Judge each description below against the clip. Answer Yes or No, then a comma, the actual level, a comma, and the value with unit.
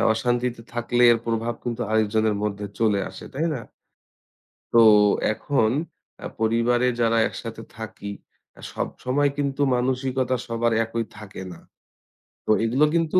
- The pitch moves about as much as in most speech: No, narrow, 2.2 semitones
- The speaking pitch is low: Yes, low, 115 Hz